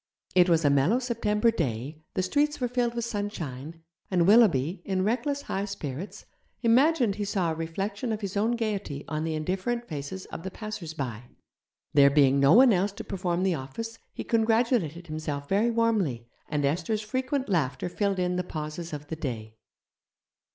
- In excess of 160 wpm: Yes, average, 170 wpm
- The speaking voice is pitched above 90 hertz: Yes, medium, 185 Hz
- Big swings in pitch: Yes, wide, 6.6 semitones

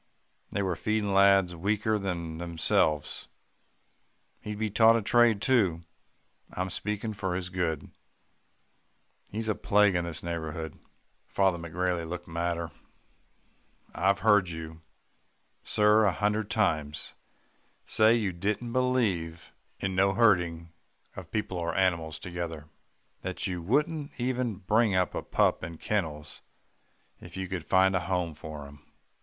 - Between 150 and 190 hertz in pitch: No, very low, 95 Hz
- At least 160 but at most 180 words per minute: No, slow, 135 wpm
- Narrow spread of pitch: No, average, 4.0 semitones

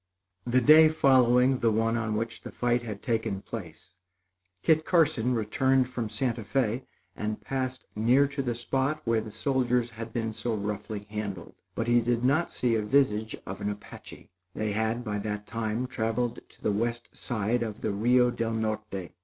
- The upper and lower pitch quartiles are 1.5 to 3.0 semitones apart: Yes, average, 2.7 semitones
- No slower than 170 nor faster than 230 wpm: Yes, average, 180 wpm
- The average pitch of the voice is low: Yes, low, 115 Hz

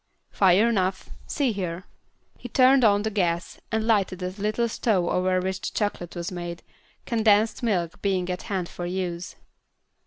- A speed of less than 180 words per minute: Yes, average, 160 wpm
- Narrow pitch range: No, average, 3.3 semitones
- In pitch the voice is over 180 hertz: Yes, high, 190 Hz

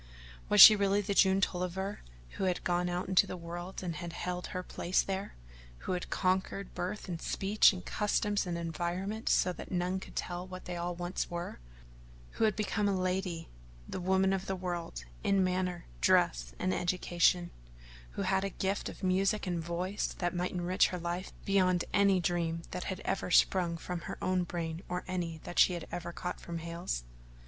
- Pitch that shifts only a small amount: Yes, narrow, 1.6 semitones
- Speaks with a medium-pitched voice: Yes, medium, 180 Hz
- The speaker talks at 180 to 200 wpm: Yes, average, 190 wpm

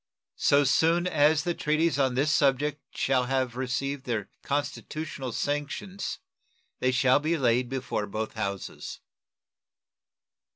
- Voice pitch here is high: No, low, 135 Hz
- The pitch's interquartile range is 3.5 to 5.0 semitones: No, average, 2.9 semitones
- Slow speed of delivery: Yes, slow, 120 wpm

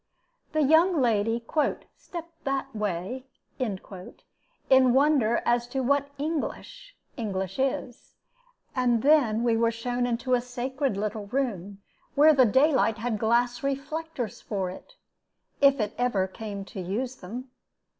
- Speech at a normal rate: No, slow, 130 wpm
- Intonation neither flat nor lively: Yes, average, 4.3 semitones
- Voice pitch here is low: No, high, 245 Hz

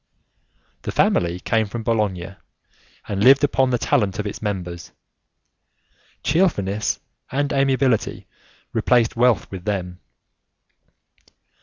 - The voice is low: Yes, low, 110 Hz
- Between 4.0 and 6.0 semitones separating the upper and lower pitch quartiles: Yes, average, 5.2 semitones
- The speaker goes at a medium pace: No, slow, 105 wpm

